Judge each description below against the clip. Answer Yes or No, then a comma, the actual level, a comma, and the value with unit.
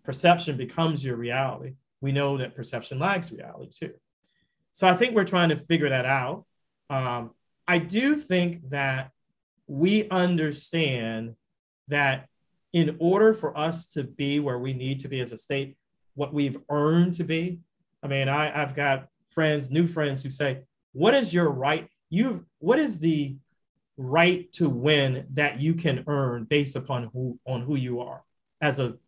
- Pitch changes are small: No, average, 4.0 semitones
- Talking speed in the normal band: Yes, average, 165 wpm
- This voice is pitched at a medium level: Yes, medium, 145 Hz